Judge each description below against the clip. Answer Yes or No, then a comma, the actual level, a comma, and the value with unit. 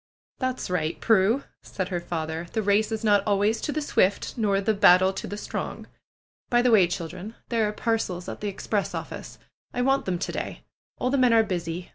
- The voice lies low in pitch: No, high, 205 Hz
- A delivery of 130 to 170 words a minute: No, fast, 205 wpm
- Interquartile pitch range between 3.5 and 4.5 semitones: Yes, average, 3.9 semitones